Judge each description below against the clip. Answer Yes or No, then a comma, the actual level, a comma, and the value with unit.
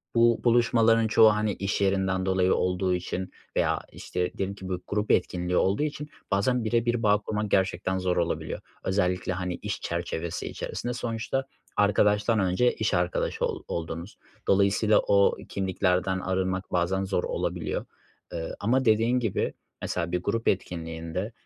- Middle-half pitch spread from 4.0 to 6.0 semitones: No, average, 3.3 semitones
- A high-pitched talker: No, very low, 95 Hz